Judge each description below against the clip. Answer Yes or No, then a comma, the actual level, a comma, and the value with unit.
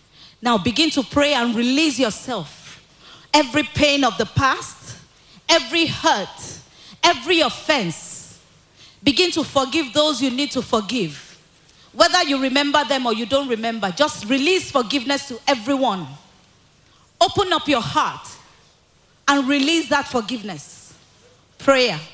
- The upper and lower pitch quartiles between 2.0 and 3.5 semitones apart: No, average, 4.2 semitones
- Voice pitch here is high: Yes, very high, 275 Hz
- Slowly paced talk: Yes, slow, 125 wpm